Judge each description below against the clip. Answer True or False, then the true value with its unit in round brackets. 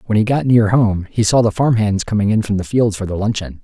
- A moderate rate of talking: False (295 wpm)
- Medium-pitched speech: False (105 Hz)